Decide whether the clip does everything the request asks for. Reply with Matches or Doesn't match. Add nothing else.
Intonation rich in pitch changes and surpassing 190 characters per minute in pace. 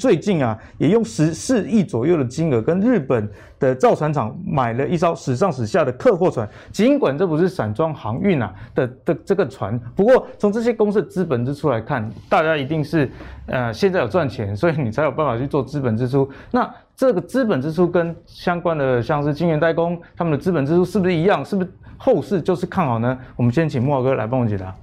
Matches